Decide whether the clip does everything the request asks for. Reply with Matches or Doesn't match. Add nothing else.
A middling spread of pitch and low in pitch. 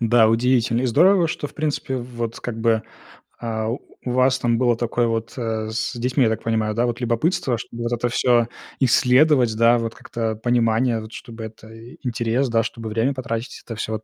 Doesn't match